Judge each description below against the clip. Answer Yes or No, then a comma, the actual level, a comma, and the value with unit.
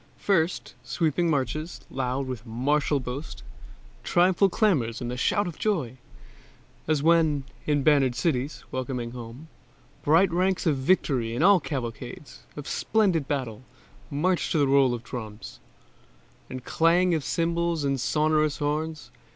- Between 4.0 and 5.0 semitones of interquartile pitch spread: Yes, average, 4.6 semitones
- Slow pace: Yes, slow, 130 wpm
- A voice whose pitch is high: No, medium, 145 Hz